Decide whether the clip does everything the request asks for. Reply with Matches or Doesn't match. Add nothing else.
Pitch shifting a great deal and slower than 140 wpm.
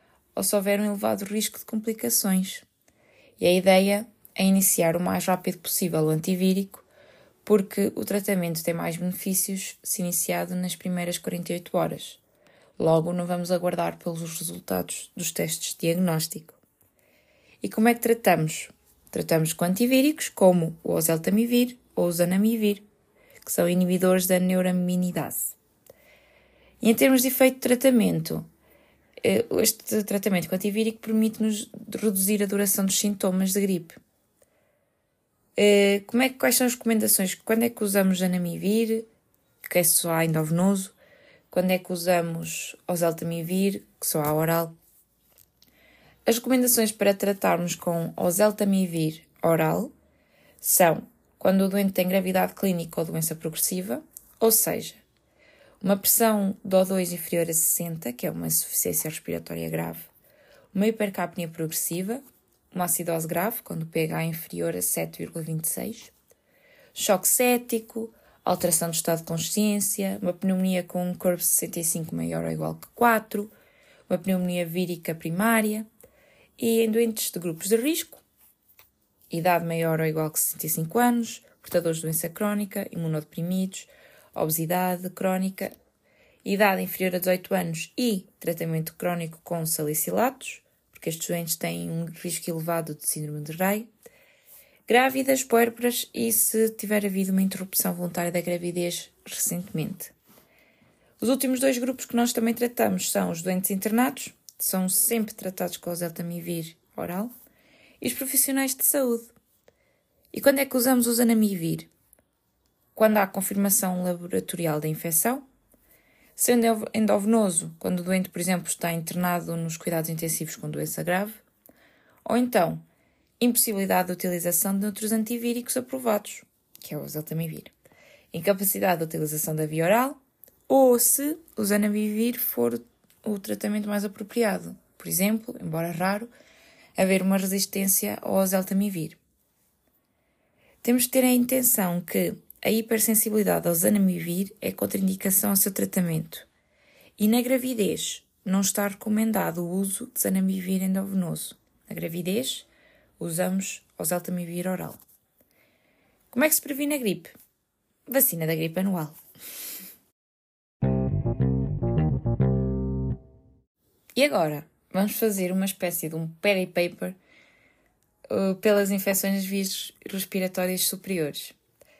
Doesn't match